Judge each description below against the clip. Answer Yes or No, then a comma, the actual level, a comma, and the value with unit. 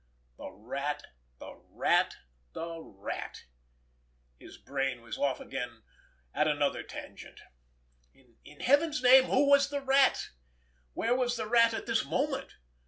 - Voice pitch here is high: Yes, high, 225 Hz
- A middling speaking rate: No, slow, 130 wpm